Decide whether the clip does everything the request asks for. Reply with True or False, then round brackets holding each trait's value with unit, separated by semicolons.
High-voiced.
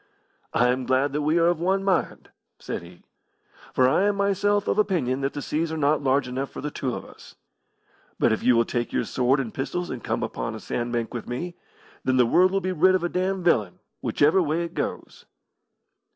False (145 Hz)